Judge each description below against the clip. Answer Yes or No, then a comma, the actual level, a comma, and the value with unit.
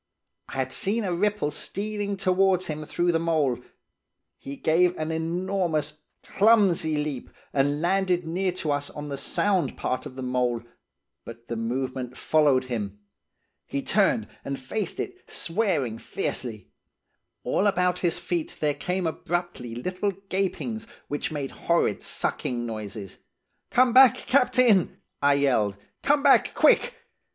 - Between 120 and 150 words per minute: Yes, average, 140 wpm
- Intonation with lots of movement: Yes, wide, 6.2 semitones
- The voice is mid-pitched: Yes, medium, 160 Hz